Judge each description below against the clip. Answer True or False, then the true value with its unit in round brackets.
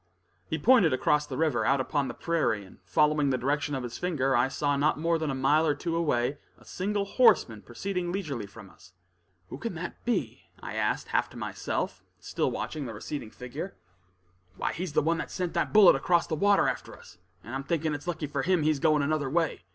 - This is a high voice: False (150 Hz)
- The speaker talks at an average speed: False (215 wpm)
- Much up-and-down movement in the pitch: False (4.1 semitones)